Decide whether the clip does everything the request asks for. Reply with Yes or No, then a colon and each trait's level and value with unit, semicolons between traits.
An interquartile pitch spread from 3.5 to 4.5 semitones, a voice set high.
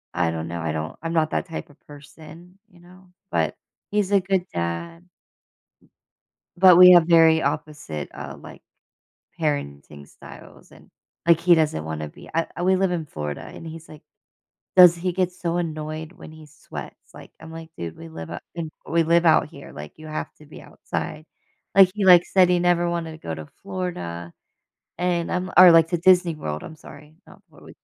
No: average, 4.1 semitones; medium, 160 Hz